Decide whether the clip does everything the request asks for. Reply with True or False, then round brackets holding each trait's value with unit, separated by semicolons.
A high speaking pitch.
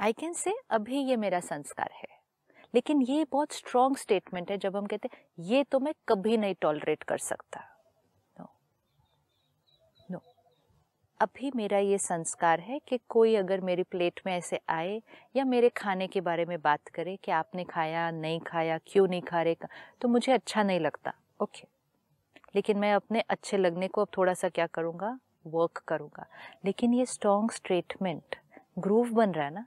True (200 Hz)